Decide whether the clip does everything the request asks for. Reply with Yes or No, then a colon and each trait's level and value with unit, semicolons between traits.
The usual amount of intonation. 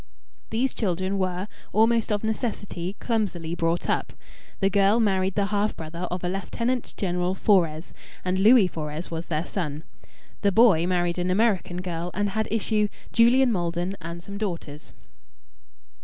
Yes: average, 3.5 semitones